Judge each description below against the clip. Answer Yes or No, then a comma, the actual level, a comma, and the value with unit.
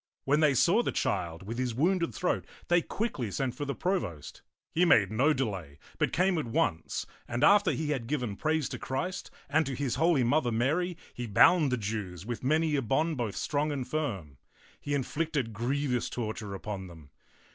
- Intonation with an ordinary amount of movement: No, wide, 6.3 semitones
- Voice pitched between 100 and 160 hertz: Yes, low, 135 Hz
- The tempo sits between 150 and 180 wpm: No, average, 190 wpm